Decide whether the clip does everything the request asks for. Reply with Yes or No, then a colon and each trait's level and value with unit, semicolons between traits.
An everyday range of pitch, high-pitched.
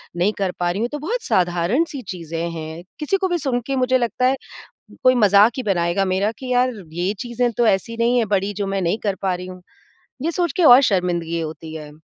No: wide, 6.1 semitones; high, 205 Hz